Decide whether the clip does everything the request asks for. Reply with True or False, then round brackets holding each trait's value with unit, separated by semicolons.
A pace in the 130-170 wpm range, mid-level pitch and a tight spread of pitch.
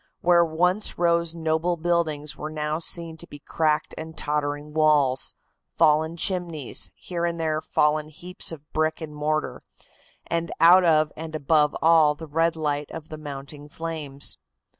True (155 wpm; 155 Hz; 1.8 semitones)